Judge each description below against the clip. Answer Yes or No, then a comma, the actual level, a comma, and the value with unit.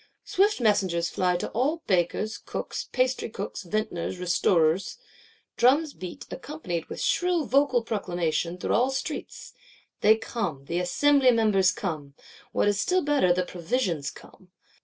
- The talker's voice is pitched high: Yes, high, 205 Hz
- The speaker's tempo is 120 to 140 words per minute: Yes, slow, 135 wpm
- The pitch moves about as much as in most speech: No, wide, 6.7 semitones